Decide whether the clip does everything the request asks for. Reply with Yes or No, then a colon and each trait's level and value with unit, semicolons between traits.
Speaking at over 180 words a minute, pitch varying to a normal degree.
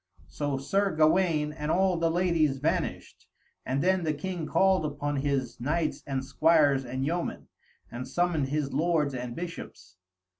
No: average, 150 wpm; average, 3.9 semitones